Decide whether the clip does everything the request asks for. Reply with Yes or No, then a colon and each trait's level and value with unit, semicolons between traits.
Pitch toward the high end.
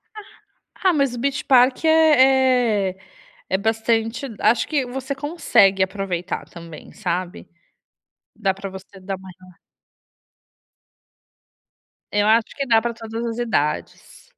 Yes: high, 225 Hz